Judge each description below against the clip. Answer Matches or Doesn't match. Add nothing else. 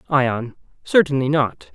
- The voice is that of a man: Matches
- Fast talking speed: Doesn't match